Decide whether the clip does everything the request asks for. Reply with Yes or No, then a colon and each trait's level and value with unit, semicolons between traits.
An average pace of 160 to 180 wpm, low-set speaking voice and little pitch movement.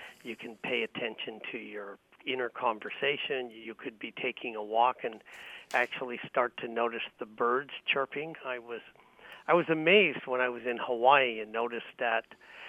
No: average, 165 wpm; low, 125 Hz; average, 3.5 semitones